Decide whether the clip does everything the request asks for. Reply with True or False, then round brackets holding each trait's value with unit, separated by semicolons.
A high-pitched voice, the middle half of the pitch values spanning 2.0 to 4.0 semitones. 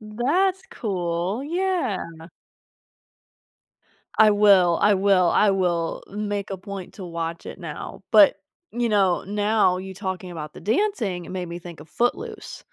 True (200 Hz; 3.7 semitones)